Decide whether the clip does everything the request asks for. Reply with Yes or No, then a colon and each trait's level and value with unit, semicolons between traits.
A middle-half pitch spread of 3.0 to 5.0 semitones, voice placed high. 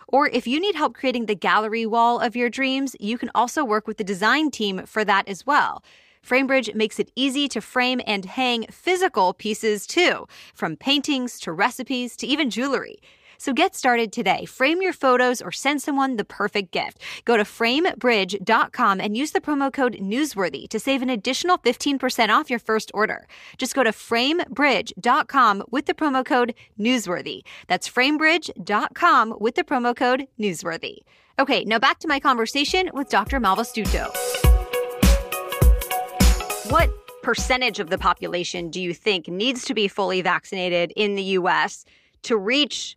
Yes: average, 4.6 semitones; high, 245 Hz